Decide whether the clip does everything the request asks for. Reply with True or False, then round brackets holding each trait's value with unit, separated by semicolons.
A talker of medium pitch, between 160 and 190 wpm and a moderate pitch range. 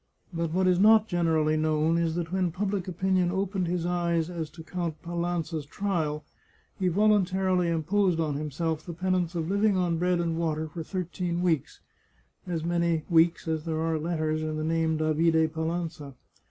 False (170 Hz; 175 wpm; 2.1 semitones)